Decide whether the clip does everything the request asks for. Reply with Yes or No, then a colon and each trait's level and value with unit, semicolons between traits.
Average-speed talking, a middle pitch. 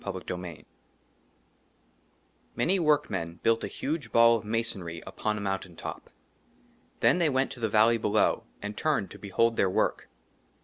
No: average, 150 wpm; low, 110 Hz